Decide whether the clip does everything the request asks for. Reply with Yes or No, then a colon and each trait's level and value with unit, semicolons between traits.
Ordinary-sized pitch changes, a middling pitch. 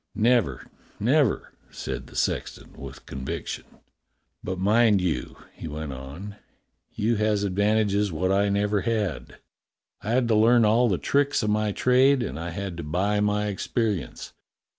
No: average, 3.7 semitones; low, 105 Hz